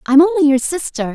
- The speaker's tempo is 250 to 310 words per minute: No, fast, 210 wpm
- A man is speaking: No, female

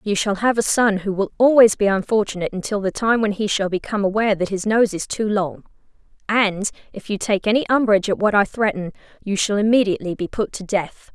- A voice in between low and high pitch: No, high, 205 Hz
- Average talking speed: No, fast, 220 wpm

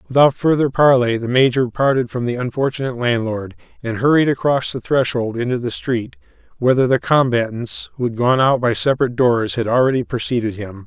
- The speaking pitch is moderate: No, low, 125 Hz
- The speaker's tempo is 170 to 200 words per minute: Yes, average, 175 wpm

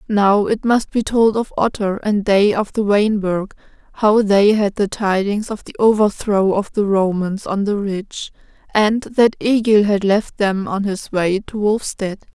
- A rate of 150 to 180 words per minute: No, average, 190 wpm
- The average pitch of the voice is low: No, high, 205 Hz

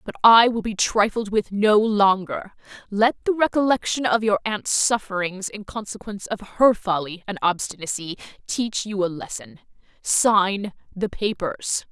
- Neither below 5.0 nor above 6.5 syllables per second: No, 4.4 syllables/s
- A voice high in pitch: Yes, high, 205 Hz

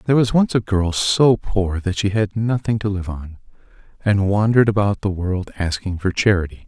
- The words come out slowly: No, average, 200 wpm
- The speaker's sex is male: Yes, male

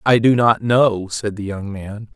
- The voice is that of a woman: No, male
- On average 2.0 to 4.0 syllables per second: Yes, 3.9 syllables/s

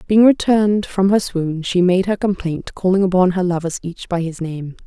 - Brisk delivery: Yes, fast, 210 wpm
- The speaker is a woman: Yes, female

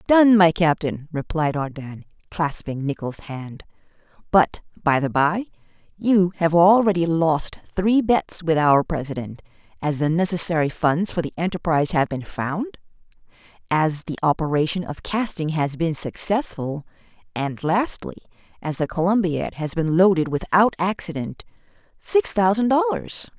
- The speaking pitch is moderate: Yes, medium, 165 Hz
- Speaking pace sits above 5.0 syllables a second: No, 4.5 syllables/s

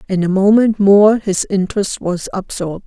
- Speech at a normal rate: Yes, average, 165 wpm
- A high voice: Yes, high, 195 Hz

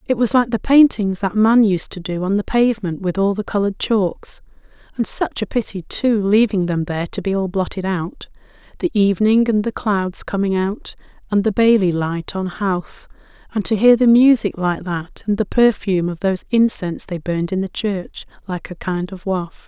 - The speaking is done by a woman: Yes, female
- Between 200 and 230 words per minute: Yes, fast, 205 wpm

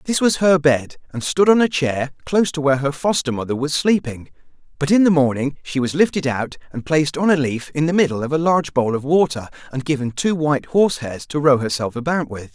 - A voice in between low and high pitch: Yes, medium, 145 Hz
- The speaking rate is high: Yes, fast, 240 wpm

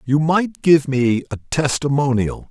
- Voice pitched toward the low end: No, medium, 145 Hz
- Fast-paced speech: No, average, 145 wpm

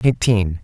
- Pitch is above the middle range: No, low, 105 Hz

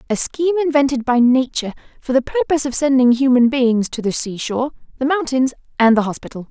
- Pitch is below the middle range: No, very high, 260 Hz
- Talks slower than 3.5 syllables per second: No, 6.2 syllables/s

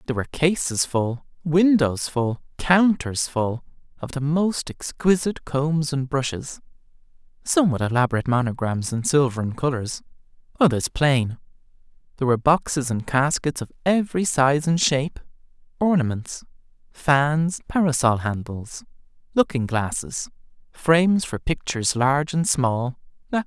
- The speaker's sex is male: Yes, male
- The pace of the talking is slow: Yes, slow, 125 wpm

